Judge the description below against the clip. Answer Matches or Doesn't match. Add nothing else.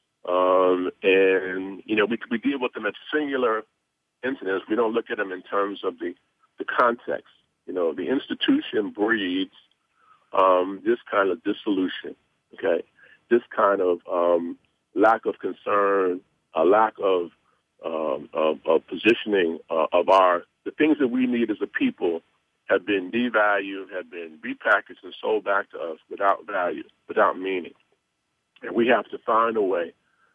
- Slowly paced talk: Doesn't match